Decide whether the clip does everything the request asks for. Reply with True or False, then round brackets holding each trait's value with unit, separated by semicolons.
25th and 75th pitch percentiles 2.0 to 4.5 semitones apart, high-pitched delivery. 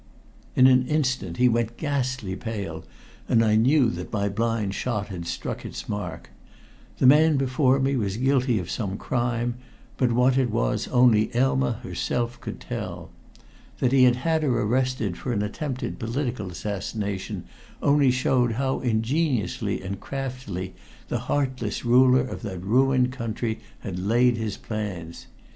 False (3.7 semitones; 120 Hz)